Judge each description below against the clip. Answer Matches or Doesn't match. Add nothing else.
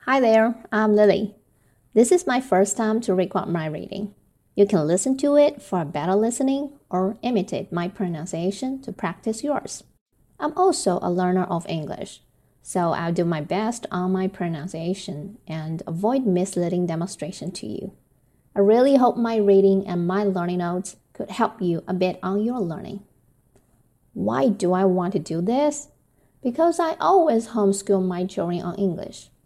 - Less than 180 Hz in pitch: Doesn't match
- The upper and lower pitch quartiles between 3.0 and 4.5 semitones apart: Matches